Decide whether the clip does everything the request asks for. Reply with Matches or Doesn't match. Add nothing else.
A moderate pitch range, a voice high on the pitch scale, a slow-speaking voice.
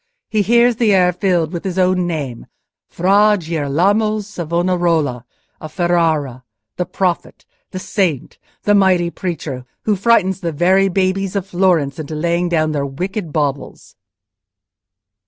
Doesn't match